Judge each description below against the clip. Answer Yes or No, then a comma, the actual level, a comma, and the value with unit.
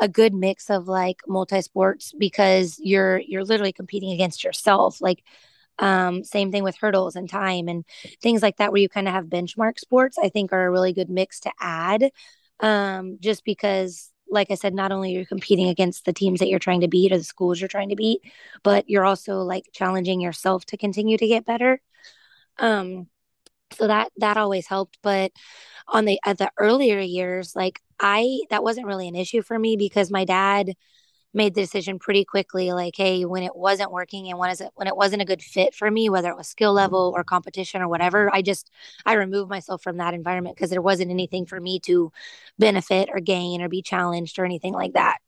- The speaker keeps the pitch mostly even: Yes, narrow, 1.9 semitones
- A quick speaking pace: Yes, fast, 210 wpm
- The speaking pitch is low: No, high, 195 Hz